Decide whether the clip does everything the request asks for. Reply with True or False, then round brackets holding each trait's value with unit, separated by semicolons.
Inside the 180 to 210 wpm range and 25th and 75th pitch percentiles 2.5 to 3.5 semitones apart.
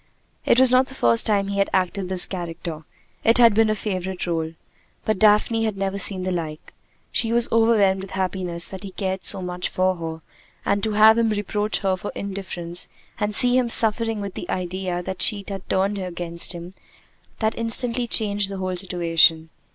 True (190 wpm; 3.2 semitones)